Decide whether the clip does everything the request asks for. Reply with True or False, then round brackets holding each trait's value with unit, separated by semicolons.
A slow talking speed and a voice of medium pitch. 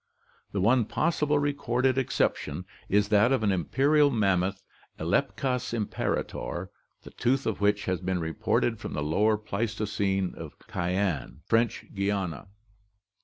False (125 wpm; 105 Hz)